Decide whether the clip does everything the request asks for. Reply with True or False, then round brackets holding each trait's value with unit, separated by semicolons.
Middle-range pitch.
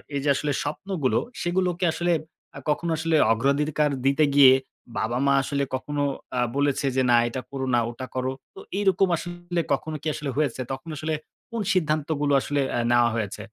True (145 Hz)